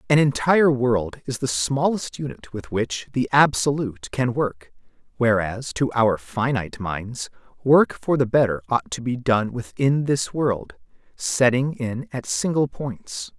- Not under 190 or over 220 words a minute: No, average, 150 wpm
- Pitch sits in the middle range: No, low, 125 Hz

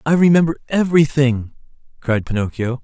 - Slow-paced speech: Yes, slow, 105 wpm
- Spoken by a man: Yes, male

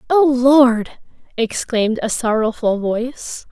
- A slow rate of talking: Yes, slow, 100 wpm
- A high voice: Yes, high, 240 Hz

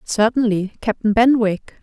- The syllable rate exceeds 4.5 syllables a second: No, 4.2 syllables/s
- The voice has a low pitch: No, high, 220 Hz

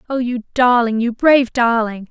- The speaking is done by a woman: Yes, female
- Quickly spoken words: No, average, 170 wpm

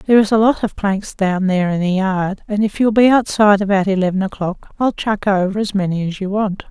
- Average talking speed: No, fast, 240 wpm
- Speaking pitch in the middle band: No, high, 200 Hz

